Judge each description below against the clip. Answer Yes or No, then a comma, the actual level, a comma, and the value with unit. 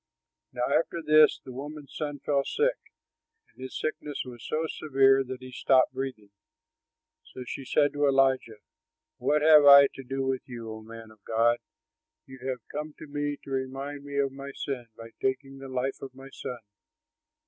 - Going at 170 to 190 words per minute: Yes, average, 180 wpm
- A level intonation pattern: Yes, narrow, 2.1 semitones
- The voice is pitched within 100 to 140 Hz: Yes, low, 135 Hz